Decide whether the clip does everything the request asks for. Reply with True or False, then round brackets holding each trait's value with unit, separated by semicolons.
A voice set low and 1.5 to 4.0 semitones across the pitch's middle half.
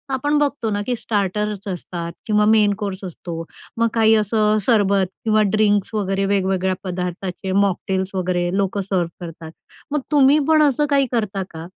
False (200 Hz; 2.8 semitones)